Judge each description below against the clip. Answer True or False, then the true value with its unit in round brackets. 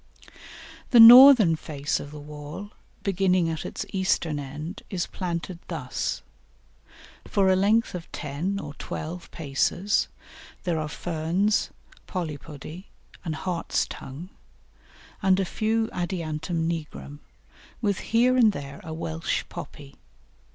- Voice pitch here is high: False (170 Hz)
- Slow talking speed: True (115 wpm)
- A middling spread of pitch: True (4.3 semitones)